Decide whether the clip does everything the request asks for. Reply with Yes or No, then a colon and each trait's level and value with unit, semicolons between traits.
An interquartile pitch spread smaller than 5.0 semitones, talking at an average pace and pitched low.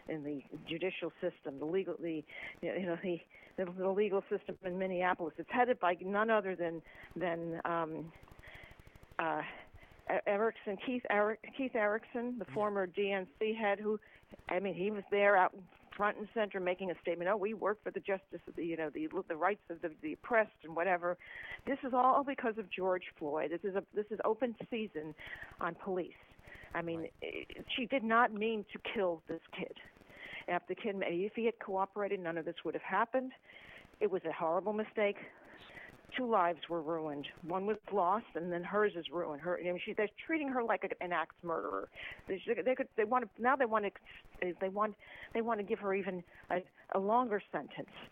No: average, 3.8 semitones; average, 190 wpm; high, 195 Hz